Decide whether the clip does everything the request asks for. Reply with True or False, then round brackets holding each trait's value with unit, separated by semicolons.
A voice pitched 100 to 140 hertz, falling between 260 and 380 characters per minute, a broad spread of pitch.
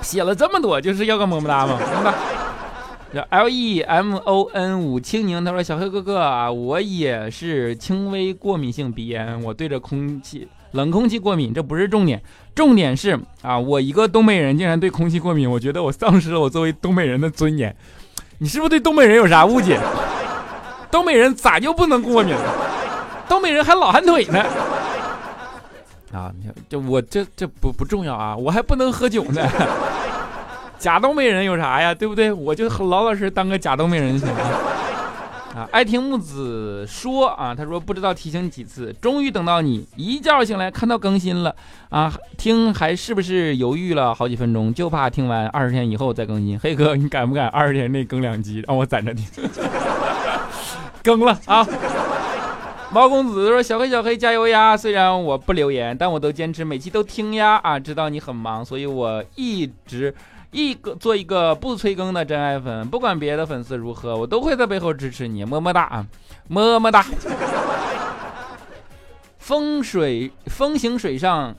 False (170 Hz; 265 characters per minute; 8.7 semitones)